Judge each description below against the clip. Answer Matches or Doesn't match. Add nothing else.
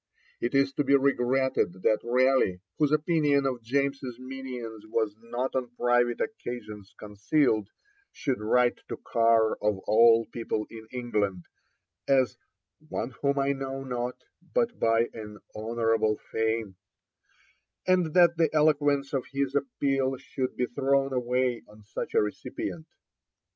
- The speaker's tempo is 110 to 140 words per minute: Matches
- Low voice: Matches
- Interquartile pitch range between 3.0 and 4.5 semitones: Matches